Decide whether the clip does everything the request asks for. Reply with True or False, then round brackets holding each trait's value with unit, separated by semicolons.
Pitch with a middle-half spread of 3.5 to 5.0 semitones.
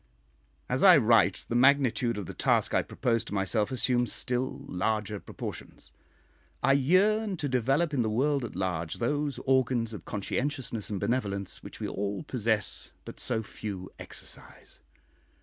True (4.6 semitones)